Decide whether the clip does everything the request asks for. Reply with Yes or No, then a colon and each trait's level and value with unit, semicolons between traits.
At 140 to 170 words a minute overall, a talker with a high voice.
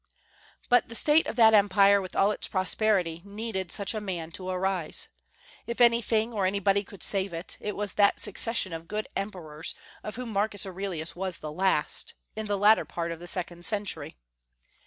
No: average, 180 wpm; high, 195 Hz